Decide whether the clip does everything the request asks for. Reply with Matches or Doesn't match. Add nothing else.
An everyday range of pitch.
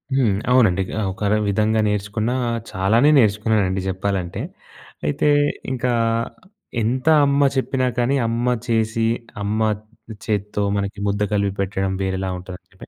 Matches